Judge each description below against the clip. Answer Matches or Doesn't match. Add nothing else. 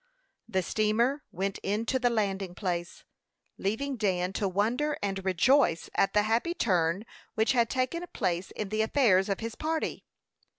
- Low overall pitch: Doesn't match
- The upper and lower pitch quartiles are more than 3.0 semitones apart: Matches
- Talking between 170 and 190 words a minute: Doesn't match